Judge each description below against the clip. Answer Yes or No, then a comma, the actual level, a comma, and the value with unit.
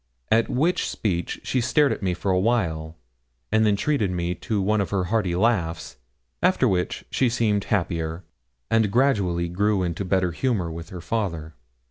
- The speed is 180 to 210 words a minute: No, average, 170 wpm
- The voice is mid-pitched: No, very low, 95 Hz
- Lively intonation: No, average, 4.6 semitones